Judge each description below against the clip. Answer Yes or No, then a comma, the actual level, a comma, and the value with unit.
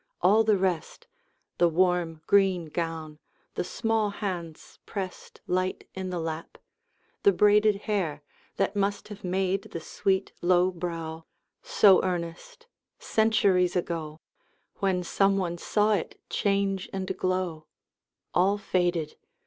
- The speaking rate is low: Yes, slow, 125 wpm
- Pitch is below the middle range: No, medium, 185 Hz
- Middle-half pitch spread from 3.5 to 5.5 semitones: No, average, 2.7 semitones